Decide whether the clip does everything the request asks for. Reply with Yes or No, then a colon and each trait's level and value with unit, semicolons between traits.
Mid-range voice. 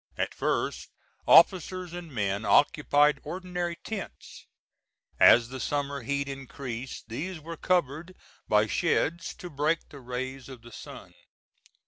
Yes: medium, 145 Hz